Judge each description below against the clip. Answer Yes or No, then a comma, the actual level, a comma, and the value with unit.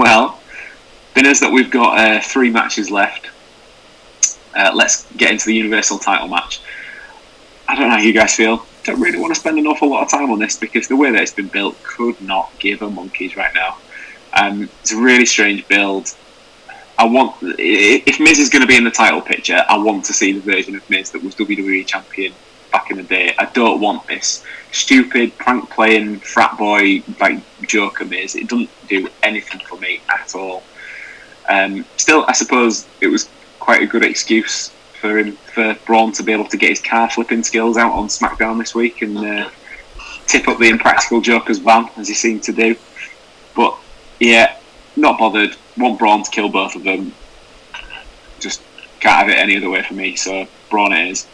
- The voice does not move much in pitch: Yes, narrow, 2.2 semitones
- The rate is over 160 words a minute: Yes, average, 195 wpm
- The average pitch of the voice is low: Yes, low, 110 Hz